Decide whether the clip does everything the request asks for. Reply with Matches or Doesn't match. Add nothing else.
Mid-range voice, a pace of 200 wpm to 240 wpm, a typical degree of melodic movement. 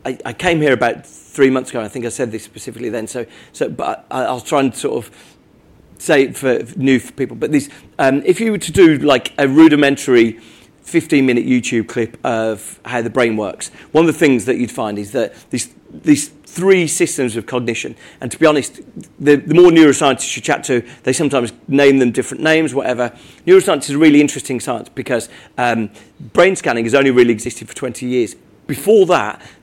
Doesn't match